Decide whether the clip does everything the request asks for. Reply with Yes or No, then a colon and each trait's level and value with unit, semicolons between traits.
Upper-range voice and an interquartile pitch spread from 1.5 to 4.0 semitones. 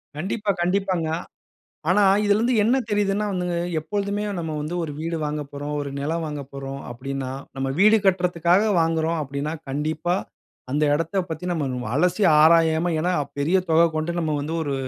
No: medium, 165 Hz; average, 3.7 semitones